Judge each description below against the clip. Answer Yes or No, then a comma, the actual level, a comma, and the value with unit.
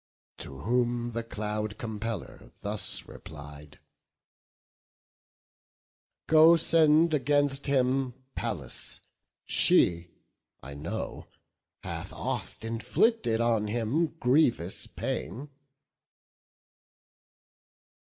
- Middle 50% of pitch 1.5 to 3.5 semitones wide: No, average, 4.8 semitones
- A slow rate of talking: Yes, slow, 75 wpm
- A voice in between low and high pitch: No, low, 115 Hz